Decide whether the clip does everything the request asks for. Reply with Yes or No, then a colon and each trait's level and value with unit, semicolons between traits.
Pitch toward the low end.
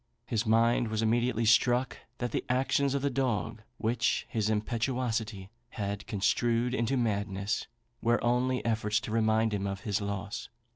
Yes: low, 115 Hz